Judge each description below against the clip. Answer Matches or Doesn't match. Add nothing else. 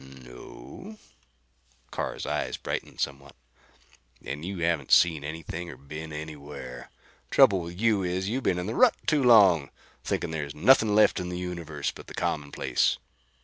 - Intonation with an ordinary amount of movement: Matches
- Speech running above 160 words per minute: Doesn't match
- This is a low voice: Matches